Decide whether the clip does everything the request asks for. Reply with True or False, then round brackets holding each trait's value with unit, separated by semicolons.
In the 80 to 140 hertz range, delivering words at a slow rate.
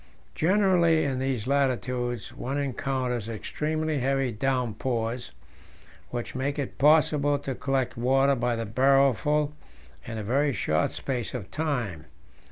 True (135 Hz; 125 wpm)